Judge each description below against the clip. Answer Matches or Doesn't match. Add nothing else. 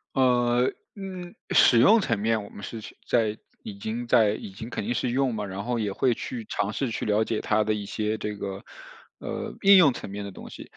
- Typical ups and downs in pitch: Matches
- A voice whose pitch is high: Doesn't match